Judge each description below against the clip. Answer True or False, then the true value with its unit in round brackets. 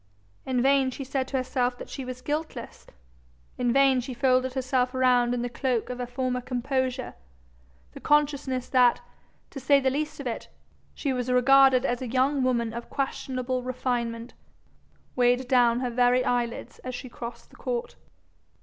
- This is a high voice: True (255 Hz)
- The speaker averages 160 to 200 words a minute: True (170 wpm)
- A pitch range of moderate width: False (1.4 semitones)